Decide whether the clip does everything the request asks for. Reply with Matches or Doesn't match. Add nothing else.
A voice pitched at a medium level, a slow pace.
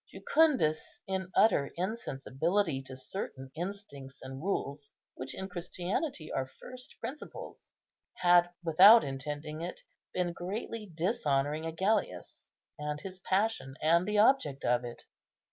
Matches